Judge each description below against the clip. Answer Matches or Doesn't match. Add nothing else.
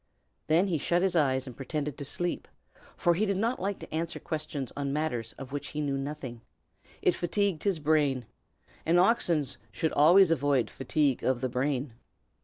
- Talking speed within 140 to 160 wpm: Doesn't match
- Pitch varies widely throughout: Doesn't match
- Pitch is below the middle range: Doesn't match